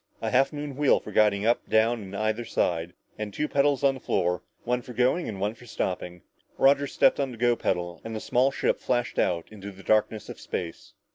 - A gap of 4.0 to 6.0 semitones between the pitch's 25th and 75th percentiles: Yes, average, 4.9 semitones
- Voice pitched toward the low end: Yes, low, 110 Hz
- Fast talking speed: Yes, fast, 220 wpm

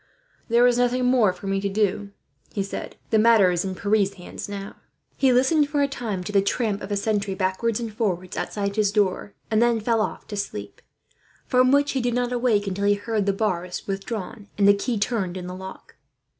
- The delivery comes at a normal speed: No, fast, 215 wpm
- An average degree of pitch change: Yes, average, 3.4 semitones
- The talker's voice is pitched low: No, high, 205 Hz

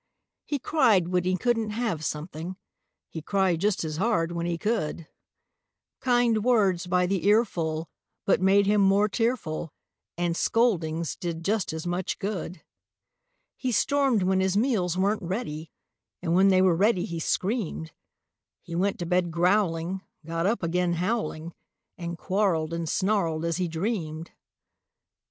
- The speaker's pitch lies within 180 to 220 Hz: Yes, medium, 185 Hz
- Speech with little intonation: No, average, 3.9 semitones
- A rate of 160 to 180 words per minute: No, average, 145 wpm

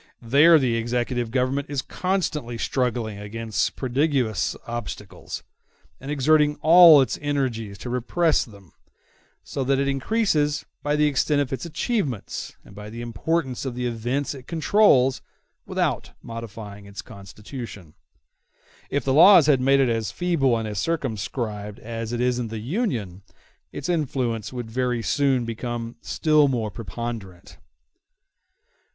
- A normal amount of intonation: Yes, average, 4.3 semitones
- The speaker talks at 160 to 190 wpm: No, average, 140 wpm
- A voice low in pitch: Yes, low, 125 Hz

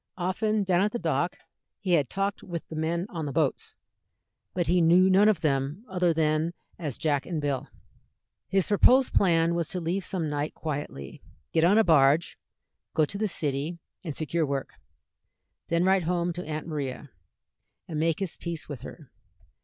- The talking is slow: No, average, 175 wpm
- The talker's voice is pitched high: No, medium, 165 Hz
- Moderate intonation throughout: Yes, average, 3.4 semitones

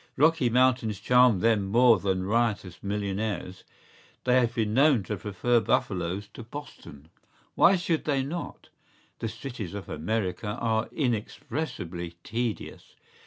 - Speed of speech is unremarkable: No, slow, 130 wpm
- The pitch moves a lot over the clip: No, average, 4.2 semitones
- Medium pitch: No, low, 110 Hz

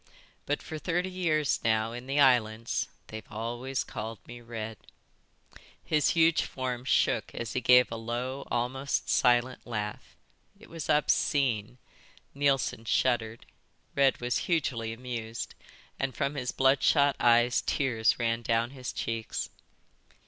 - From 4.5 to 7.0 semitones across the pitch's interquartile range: No, average, 3.2 semitones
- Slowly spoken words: Yes, slow, 130 wpm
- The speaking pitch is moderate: No, low, 125 Hz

